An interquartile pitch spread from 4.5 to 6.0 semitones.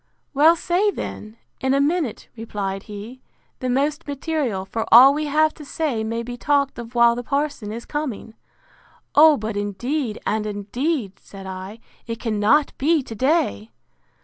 Yes: wide, 5.6 semitones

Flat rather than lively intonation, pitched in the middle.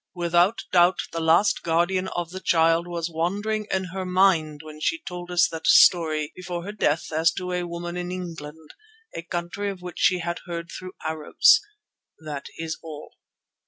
Yes: narrow, 2.1 semitones; medium, 175 Hz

